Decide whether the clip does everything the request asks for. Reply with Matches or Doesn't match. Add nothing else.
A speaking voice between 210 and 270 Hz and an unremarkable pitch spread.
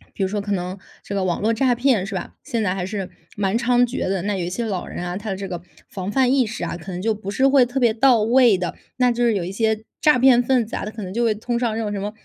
Matches